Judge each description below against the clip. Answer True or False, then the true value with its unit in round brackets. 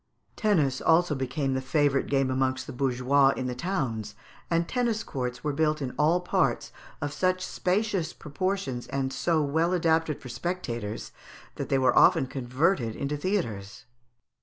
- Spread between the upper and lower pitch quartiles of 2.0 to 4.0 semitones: False (4.8 semitones)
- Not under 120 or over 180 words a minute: True (160 wpm)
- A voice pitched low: False (145 Hz)